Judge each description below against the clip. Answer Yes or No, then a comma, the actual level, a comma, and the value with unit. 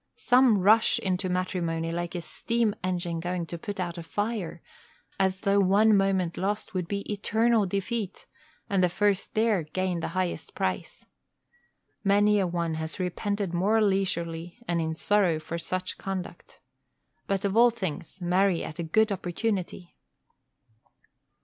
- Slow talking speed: No, average, 150 wpm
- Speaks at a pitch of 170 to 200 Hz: Yes, medium, 185 Hz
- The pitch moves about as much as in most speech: Yes, average, 3.0 semitones